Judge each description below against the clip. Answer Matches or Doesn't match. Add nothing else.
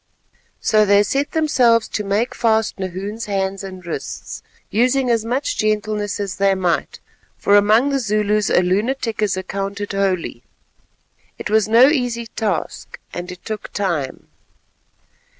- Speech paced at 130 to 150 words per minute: Matches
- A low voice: Doesn't match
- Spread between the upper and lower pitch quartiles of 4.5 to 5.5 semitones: Doesn't match